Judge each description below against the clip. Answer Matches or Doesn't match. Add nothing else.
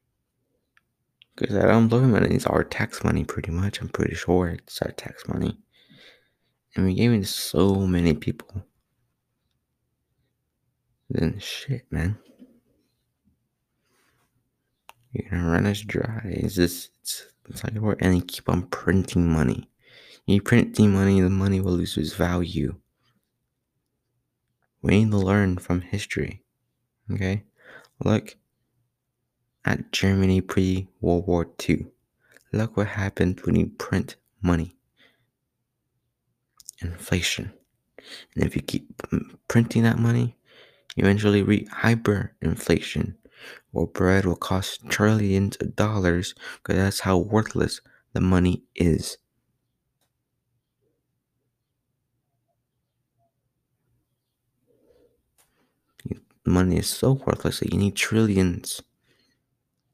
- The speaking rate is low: Matches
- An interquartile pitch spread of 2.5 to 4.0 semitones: Doesn't match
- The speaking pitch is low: Matches